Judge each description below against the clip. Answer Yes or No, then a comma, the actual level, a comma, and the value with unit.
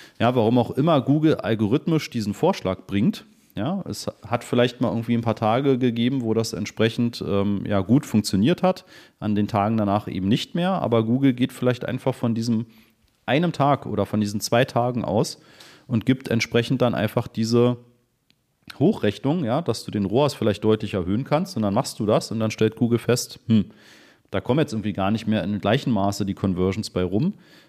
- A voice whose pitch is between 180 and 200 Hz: No, low, 115 Hz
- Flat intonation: No, average, 3.2 semitones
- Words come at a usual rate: No, fast, 195 wpm